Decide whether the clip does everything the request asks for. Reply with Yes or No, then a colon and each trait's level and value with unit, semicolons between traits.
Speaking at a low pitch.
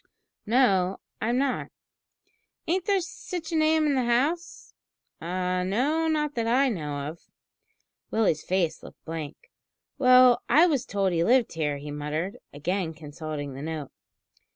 No: high, 200 Hz